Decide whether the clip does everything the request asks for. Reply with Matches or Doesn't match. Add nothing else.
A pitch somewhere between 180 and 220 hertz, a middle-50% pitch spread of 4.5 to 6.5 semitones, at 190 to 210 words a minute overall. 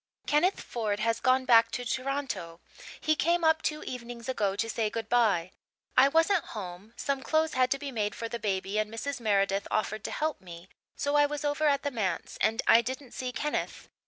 Doesn't match